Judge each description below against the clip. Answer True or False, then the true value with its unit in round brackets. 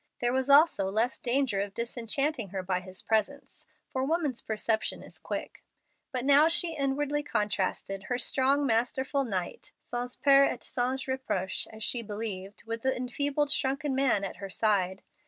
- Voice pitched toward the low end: False (245 Hz)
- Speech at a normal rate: True (160 wpm)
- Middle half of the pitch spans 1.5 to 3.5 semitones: False (4.8 semitones)